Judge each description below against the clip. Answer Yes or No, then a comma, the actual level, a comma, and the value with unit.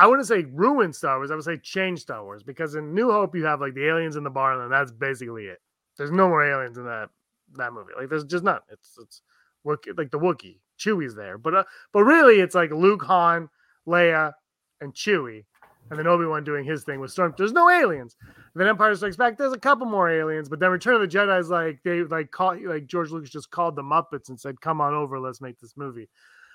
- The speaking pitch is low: No, medium, 160 Hz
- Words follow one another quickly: Yes, fast, 240 wpm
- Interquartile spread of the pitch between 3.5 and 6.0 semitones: Yes, average, 4.6 semitones